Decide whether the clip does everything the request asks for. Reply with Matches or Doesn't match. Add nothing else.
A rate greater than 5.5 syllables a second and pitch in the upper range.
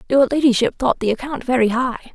Matches